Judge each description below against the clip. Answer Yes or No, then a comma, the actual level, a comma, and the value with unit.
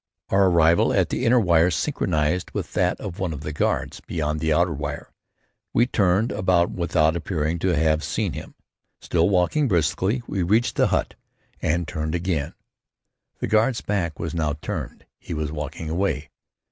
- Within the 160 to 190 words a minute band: Yes, average, 170 wpm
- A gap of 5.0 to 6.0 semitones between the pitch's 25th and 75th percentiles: No, average, 3.3 semitones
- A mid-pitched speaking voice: No, very low, 85 Hz